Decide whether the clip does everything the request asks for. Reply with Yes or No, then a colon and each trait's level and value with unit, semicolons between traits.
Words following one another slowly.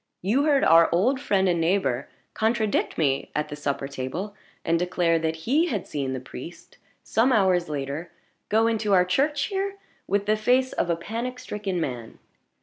No: average, 175 wpm